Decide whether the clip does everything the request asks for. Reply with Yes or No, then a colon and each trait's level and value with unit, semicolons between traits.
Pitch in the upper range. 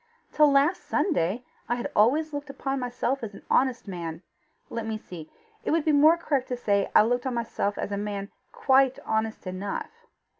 Yes: high, 245 Hz